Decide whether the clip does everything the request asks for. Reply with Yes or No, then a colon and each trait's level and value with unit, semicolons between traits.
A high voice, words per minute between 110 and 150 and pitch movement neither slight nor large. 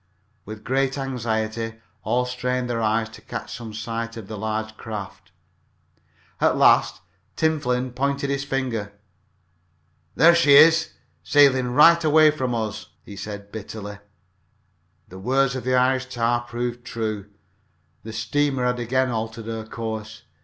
No: low, 120 Hz; average, 145 wpm; average, 3.2 semitones